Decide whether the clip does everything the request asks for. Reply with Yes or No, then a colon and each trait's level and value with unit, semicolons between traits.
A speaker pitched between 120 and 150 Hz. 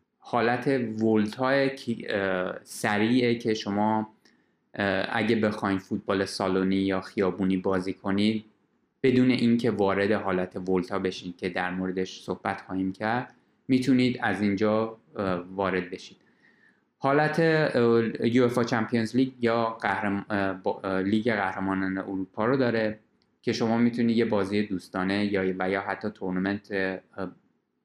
No: low, 105 Hz